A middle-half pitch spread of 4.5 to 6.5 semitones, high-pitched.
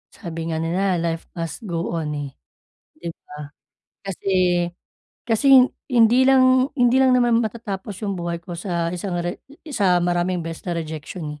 No: average, 5.2 semitones; medium, 180 Hz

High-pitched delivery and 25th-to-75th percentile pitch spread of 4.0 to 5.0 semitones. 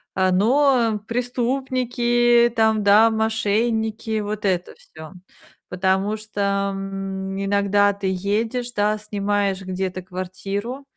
No: high, 205 Hz; average, 2.9 semitones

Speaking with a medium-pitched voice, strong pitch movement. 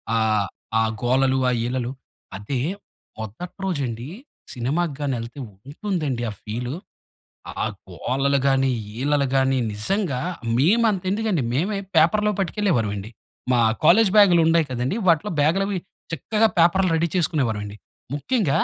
Yes: medium, 145 Hz; wide, 7.0 semitones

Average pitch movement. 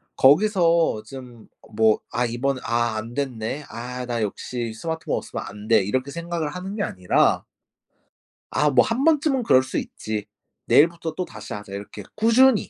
No: wide, 7.2 semitones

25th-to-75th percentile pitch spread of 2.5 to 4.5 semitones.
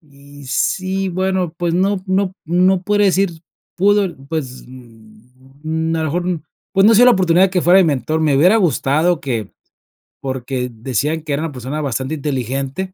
No: wide, 5.5 semitones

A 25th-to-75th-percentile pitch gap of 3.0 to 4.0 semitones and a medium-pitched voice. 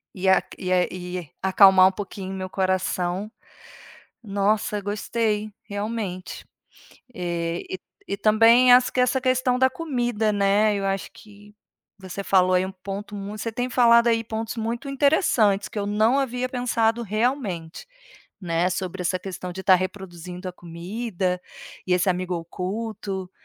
No: average, 3.7 semitones; high, 200 Hz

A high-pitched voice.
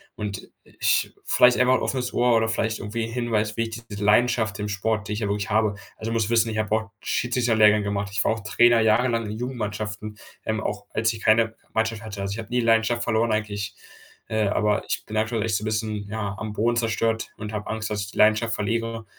No: low, 110 Hz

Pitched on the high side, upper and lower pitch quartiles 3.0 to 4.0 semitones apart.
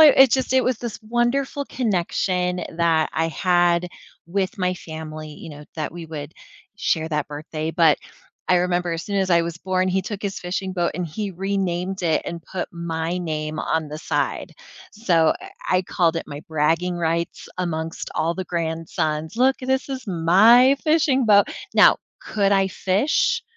No: medium, 180 Hz; average, 3.7 semitones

